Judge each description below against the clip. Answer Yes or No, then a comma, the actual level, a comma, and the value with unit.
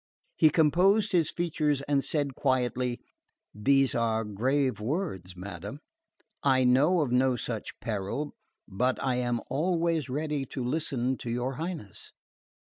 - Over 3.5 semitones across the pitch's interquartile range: Yes, average, 3.9 semitones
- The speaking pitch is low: Yes, low, 130 Hz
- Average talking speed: No, slow, 130 wpm